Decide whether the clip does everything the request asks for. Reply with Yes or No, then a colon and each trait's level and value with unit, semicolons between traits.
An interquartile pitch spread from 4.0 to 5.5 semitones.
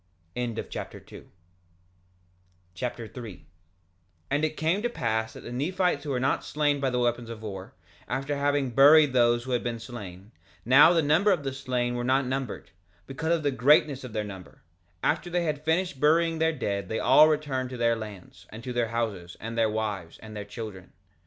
Yes: average, 4.8 semitones